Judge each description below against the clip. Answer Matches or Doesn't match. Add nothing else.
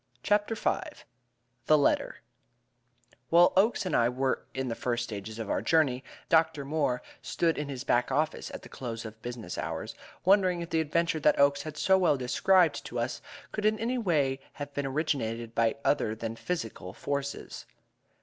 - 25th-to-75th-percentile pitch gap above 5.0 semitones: Matches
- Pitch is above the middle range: Doesn't match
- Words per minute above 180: Doesn't match